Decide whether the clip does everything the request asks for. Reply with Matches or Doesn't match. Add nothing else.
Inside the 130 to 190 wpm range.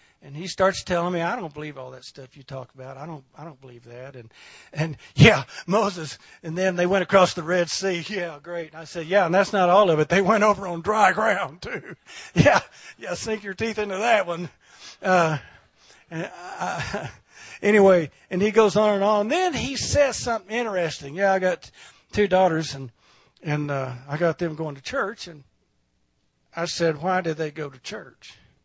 Doesn't match